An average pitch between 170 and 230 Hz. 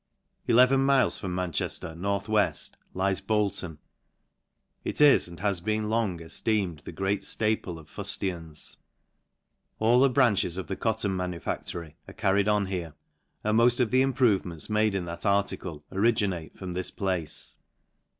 No: low, 100 Hz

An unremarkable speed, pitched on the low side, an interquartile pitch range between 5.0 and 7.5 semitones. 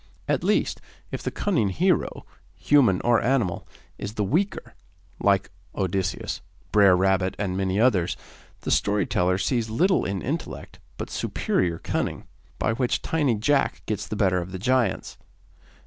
Yes: average, 150 wpm; low, 105 Hz; average, 5.3 semitones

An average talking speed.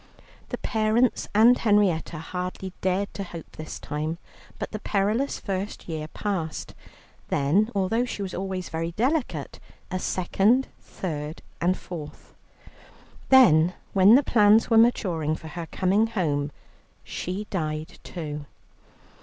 No: slow, 130 wpm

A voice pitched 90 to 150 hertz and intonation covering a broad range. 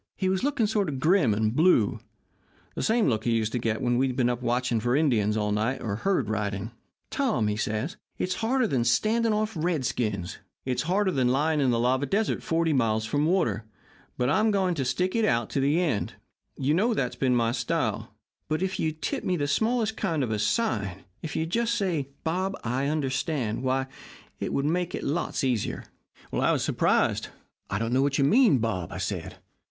Yes: medium, 140 Hz; wide, 7.7 semitones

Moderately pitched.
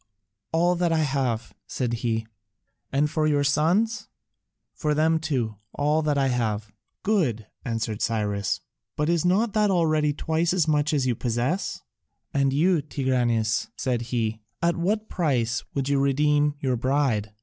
Yes: medium, 145 Hz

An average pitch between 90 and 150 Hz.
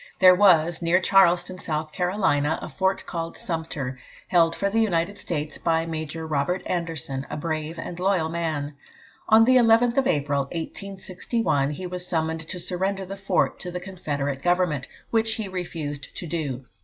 No: medium, 170 Hz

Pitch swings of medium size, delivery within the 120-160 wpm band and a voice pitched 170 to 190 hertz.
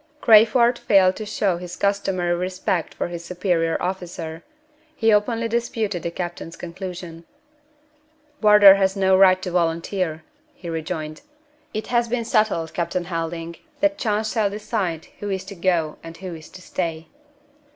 Yes: average, 3.6 semitones; average, 150 wpm; medium, 185 Hz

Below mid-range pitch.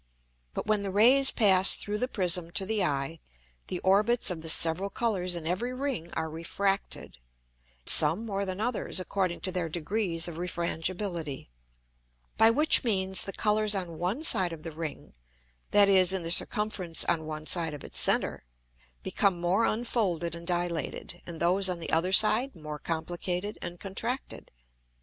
No: medium, 185 Hz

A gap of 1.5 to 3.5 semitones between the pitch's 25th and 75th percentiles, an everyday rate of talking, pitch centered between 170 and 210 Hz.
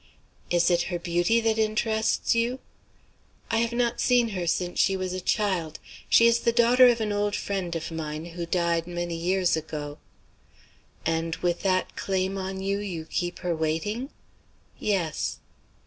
No: average, 4.3 semitones; average, 165 wpm; medium, 185 Hz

